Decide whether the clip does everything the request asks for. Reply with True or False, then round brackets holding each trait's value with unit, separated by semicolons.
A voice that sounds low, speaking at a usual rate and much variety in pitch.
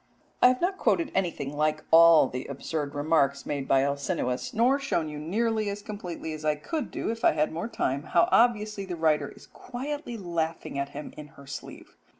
False (160 Hz; 195 wpm; 6.9 semitones)